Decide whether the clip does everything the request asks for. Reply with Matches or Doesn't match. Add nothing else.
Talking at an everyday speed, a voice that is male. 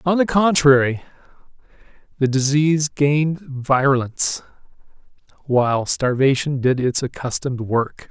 Doesn't match